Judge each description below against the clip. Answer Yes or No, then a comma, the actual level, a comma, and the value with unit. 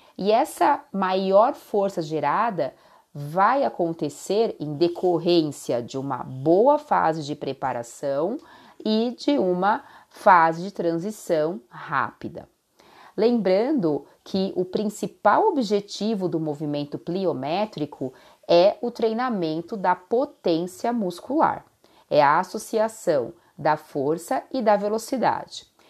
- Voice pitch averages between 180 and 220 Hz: Yes, medium, 185 Hz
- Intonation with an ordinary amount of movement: No, wide, 5.8 semitones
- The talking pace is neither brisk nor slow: No, slow, 100 wpm